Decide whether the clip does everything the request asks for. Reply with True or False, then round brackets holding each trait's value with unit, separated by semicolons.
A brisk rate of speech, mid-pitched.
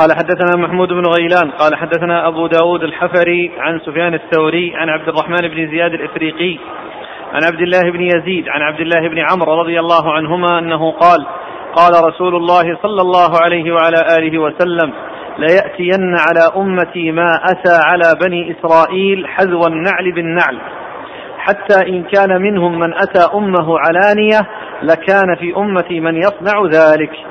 True (150 wpm; 170 Hz)